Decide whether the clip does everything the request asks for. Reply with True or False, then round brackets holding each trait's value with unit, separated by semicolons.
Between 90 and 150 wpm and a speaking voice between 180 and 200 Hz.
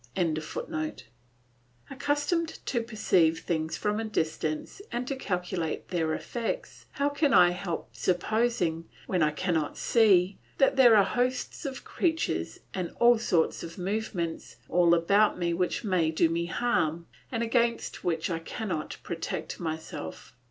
True (140 wpm; 185 Hz)